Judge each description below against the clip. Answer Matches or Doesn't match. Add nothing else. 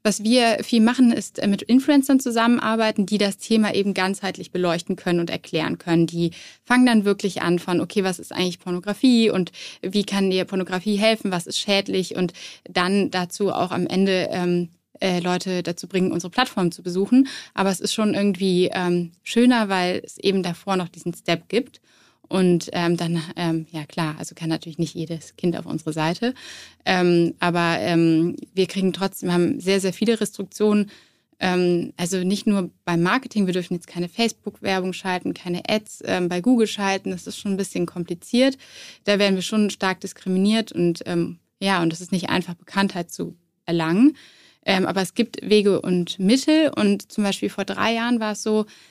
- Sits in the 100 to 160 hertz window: Doesn't match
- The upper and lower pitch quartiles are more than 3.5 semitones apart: Doesn't match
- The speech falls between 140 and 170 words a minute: Doesn't match